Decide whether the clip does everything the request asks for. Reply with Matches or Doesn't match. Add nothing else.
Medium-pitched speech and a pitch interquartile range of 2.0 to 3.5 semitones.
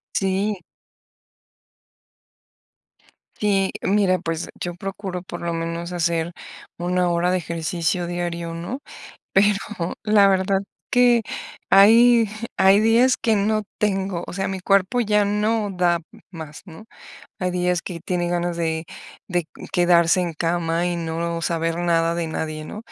Matches